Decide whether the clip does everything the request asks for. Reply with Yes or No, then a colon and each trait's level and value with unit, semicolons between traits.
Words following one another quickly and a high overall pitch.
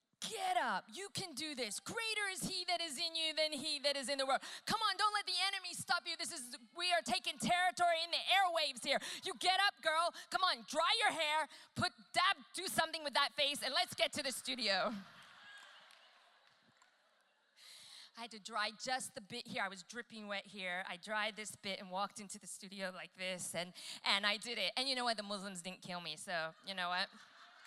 Yes: fast, 220 wpm; very high, 275 Hz